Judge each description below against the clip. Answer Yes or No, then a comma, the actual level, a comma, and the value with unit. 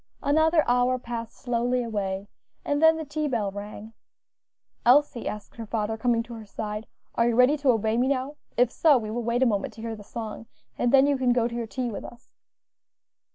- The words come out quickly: Yes, fast, 210 wpm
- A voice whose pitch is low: No, high, 235 Hz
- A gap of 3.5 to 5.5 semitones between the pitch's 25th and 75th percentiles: No, average, 2.8 semitones